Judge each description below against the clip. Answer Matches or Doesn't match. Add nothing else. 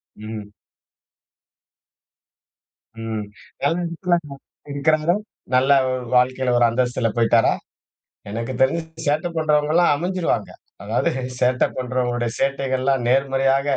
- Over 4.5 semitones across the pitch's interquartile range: Doesn't match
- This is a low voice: Matches